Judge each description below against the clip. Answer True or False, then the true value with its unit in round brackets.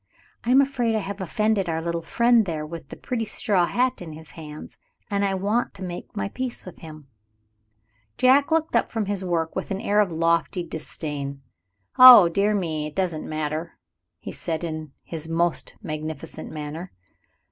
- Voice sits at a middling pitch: True (175 Hz)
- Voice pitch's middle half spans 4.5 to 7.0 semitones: True (5.0 semitones)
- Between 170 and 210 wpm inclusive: True (180 wpm)